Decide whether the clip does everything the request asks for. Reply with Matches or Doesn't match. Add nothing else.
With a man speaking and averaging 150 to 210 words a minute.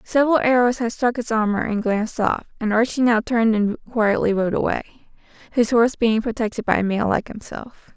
Doesn't match